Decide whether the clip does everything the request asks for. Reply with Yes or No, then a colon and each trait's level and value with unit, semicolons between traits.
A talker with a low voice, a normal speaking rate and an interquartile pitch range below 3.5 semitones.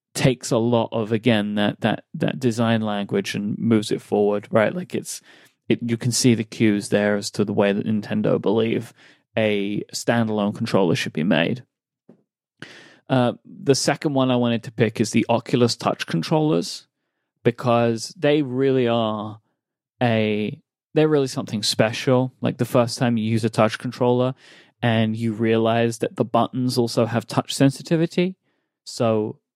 Yes: low, 120 Hz; average, 160 wpm; average, 2.8 semitones